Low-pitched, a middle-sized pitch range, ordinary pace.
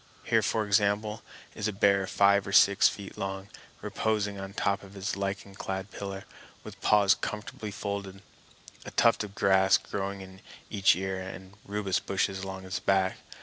No: low, 100 Hz; narrow, 0.9 semitones; average, 165 wpm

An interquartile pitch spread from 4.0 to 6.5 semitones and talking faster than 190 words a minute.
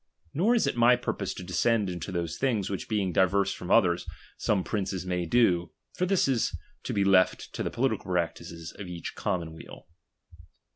No: average, 4.3 semitones; average, 180 wpm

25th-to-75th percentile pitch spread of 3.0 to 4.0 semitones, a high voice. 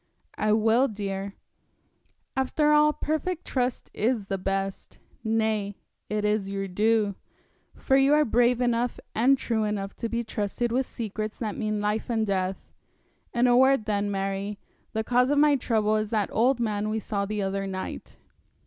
Yes: average, 3.3 semitones; high, 220 Hz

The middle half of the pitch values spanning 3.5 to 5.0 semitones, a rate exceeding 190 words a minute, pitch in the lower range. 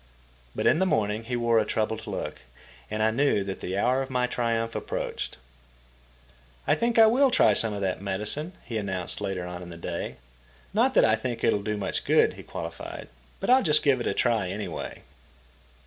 Yes: average, 4.4 semitones; average, 200 wpm; low, 110 Hz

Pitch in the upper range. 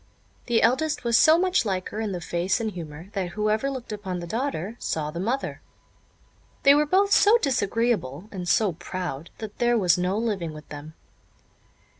Yes: high, 210 Hz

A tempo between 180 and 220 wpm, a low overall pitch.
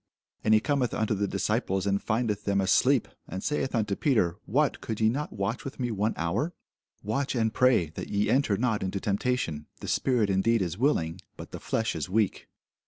Yes: average, 195 wpm; low, 110 Hz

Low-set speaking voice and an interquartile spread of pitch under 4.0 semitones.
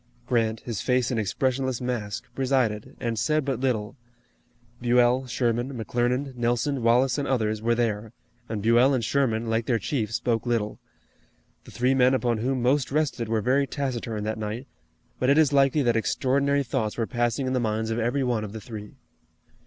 Yes: low, 120 Hz; average, 2.7 semitones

